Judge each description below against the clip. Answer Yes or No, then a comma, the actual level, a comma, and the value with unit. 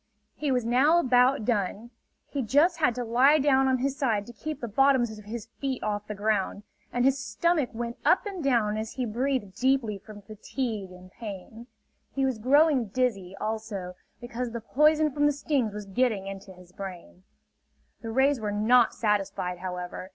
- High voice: Yes, high, 235 Hz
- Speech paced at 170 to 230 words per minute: Yes, average, 180 wpm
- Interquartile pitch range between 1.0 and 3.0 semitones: No, average, 4.5 semitones